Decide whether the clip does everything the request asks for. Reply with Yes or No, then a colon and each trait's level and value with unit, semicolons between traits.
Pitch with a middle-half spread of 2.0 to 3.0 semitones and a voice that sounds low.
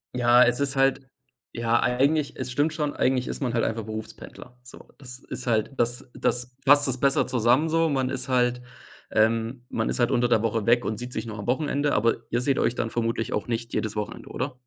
Yes: narrow, 2.5 semitones; low, 125 Hz